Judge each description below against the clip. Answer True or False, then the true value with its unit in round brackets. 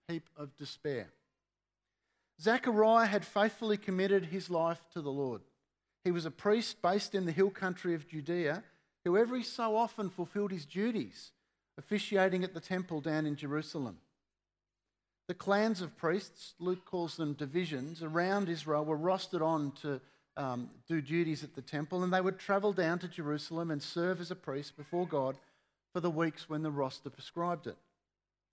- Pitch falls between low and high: True (170 Hz)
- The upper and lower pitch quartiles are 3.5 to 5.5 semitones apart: True (4.0 semitones)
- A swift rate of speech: False (165 wpm)